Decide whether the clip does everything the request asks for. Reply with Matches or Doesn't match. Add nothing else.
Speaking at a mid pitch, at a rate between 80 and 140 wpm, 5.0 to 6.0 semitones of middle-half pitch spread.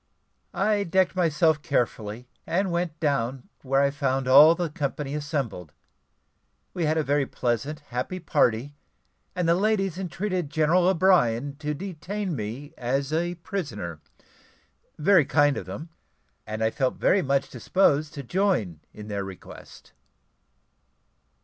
Matches